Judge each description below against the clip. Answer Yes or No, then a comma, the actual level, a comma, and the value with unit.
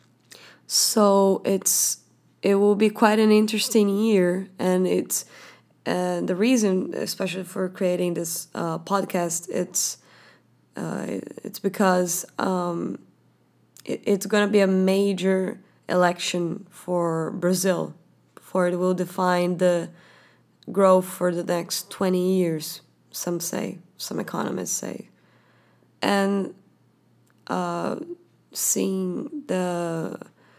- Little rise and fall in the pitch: Yes, narrow, 1.9 semitones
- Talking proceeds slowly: Yes, slow, 110 wpm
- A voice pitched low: No, medium, 185 Hz